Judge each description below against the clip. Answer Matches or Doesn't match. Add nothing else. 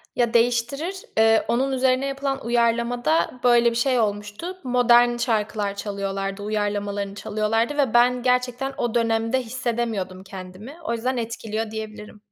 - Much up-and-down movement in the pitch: Doesn't match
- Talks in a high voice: Matches